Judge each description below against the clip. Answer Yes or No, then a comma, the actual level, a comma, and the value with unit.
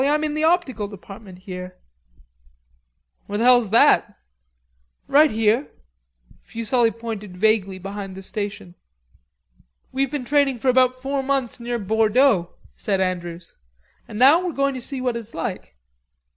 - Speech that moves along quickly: No, slow, 135 wpm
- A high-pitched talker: Yes, high, 230 Hz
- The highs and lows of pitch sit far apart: No, average, 5.0 semitones